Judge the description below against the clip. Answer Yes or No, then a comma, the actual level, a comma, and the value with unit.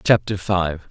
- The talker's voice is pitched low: Yes, very low, 95 Hz